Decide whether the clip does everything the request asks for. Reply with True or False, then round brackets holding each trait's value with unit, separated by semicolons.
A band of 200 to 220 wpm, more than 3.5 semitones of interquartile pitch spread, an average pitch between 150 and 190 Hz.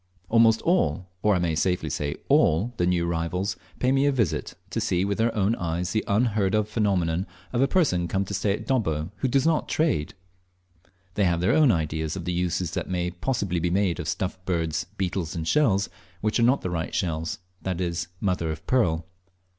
False (205 wpm; 4.3 semitones; 95 Hz)